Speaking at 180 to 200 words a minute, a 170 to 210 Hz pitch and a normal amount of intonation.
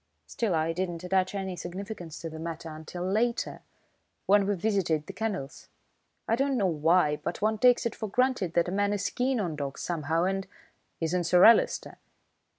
Yes: average, 185 wpm; medium, 185 Hz; average, 3.9 semitones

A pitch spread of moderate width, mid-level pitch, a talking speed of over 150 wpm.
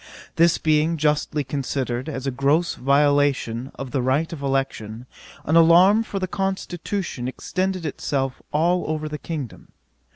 No: average, 3.8 semitones; medium, 150 Hz; average, 140 wpm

